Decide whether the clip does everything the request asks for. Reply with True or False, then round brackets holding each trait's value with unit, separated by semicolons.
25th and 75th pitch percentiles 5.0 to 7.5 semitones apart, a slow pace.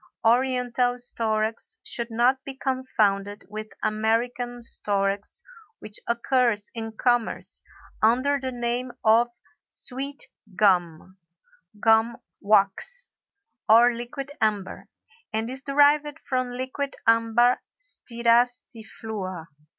False (2.8 semitones; 90 wpm)